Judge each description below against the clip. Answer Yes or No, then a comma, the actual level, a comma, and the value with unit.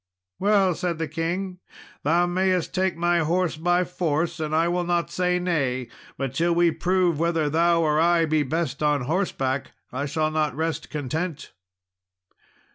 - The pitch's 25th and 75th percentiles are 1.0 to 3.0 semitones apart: Yes, narrow, 2.5 semitones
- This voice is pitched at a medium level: Yes, medium, 165 Hz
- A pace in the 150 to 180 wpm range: Yes, average, 160 wpm